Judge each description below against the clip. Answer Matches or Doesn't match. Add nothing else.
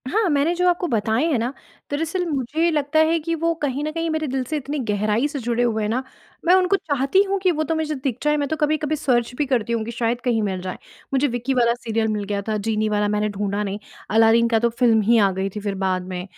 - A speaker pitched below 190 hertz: Doesn't match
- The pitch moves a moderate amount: Doesn't match